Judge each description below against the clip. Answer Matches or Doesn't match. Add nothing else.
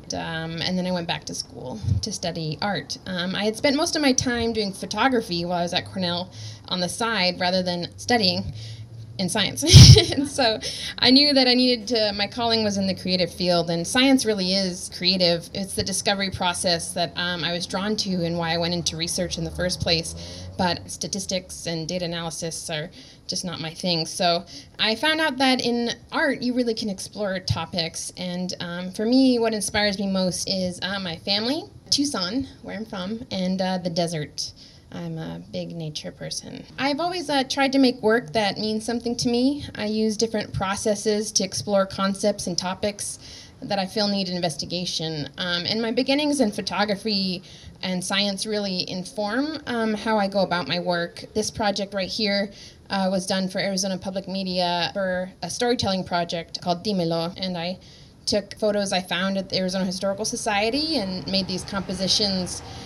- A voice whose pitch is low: Doesn't match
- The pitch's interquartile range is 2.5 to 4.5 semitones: Matches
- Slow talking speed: Doesn't match